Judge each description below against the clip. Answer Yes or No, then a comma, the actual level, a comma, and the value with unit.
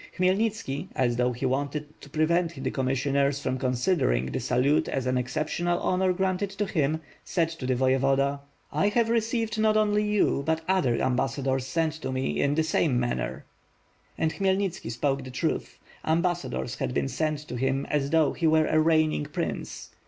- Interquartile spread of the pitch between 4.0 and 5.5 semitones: Yes, average, 5.2 semitones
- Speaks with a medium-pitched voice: Yes, medium, 150 Hz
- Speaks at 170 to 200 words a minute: Yes, average, 180 wpm